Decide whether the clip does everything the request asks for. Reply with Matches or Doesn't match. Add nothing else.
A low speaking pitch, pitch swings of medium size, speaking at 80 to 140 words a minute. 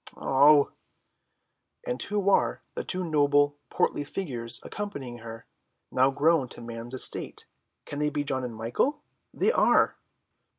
Doesn't match